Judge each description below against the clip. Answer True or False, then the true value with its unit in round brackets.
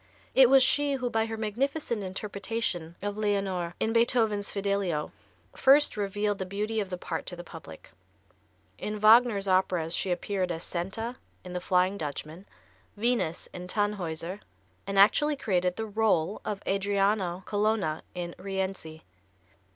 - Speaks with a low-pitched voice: False (200 Hz)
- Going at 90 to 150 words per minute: True (145 wpm)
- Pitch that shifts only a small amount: False (3.5 semitones)